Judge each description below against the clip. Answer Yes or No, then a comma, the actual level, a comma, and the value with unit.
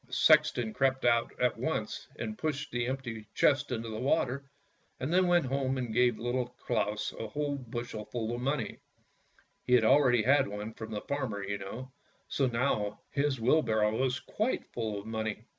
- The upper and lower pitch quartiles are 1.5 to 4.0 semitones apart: Yes, average, 3.5 semitones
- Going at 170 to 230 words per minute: Yes, average, 180 wpm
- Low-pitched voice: Yes, low, 120 Hz